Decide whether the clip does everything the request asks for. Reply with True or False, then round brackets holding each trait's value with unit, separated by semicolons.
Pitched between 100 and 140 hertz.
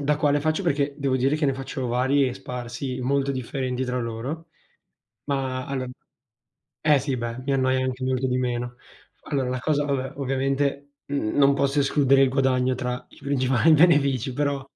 True (135 Hz)